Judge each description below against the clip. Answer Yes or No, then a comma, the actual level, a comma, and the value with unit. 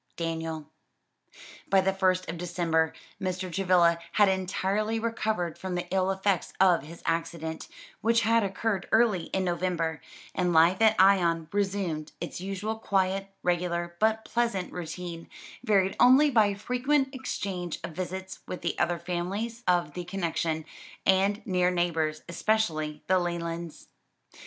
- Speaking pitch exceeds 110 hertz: Yes, medium, 185 Hz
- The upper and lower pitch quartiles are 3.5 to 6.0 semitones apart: No, average, 3.0 semitones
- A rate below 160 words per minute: Yes, slow, 135 wpm